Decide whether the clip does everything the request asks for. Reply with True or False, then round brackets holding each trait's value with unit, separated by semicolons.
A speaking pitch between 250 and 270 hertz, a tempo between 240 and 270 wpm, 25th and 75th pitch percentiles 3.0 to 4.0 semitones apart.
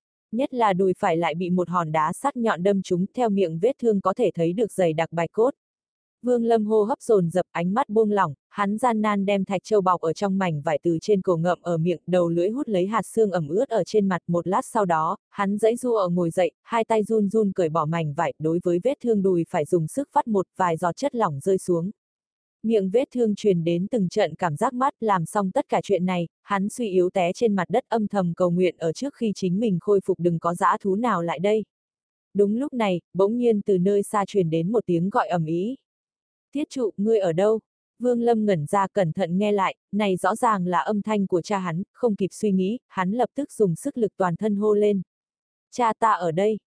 False (195 Hz; 250 wpm; 3.7 semitones)